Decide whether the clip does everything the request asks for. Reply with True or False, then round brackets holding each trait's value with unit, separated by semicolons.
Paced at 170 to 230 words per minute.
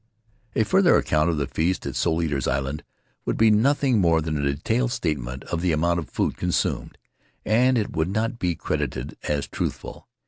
True (185 wpm)